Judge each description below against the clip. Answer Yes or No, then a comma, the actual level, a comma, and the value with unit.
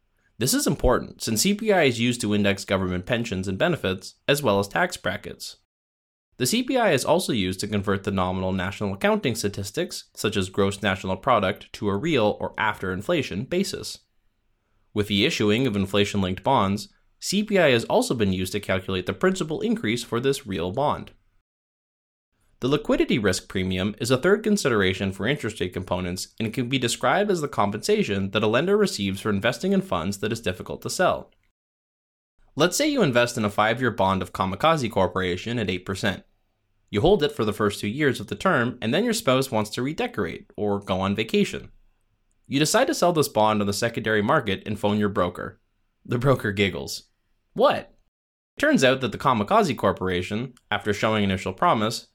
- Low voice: Yes, low, 105 Hz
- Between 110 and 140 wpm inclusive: No, average, 180 wpm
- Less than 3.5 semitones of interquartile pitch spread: No, average, 4.2 semitones